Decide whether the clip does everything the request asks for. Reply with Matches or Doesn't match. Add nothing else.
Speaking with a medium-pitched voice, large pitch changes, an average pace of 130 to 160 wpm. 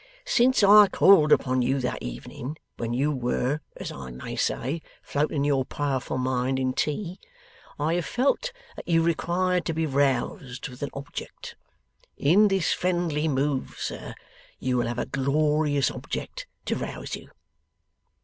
Doesn't match